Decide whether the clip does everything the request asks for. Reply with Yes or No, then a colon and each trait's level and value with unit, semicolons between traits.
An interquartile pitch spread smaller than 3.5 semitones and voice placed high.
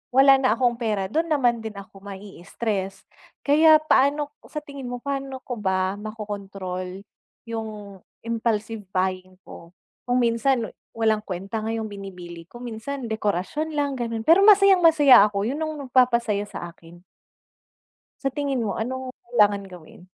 No: average, 5.2 semitones; high, 225 Hz